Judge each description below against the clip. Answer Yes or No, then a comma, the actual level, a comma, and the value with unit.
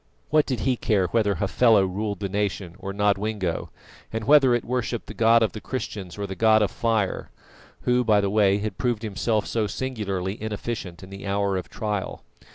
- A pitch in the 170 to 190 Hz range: No, low, 105 Hz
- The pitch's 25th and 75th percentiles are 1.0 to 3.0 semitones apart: Yes, average, 2.7 semitones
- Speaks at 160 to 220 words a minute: Yes, average, 190 wpm